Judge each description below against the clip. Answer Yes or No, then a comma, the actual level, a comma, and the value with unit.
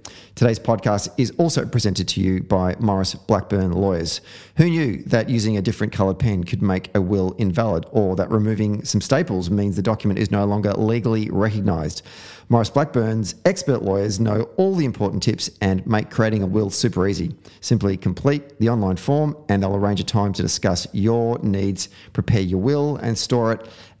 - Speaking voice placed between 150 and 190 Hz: No, low, 105 Hz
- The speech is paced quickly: No, average, 185 wpm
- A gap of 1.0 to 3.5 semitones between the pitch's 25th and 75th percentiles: Yes, average, 3.1 semitones